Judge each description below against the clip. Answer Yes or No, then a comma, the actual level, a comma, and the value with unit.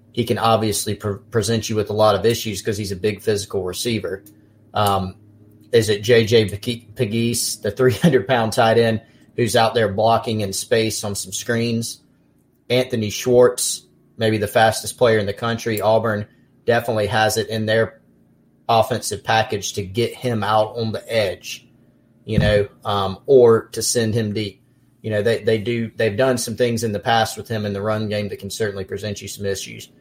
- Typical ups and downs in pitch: No, narrow, 1.9 semitones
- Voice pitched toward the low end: Yes, low, 110 Hz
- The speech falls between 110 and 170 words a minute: No, average, 185 wpm